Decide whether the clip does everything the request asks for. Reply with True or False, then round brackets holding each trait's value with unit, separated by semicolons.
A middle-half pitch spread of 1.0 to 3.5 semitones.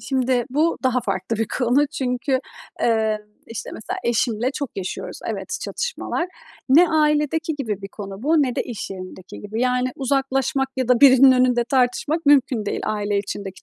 False (3.9 semitones)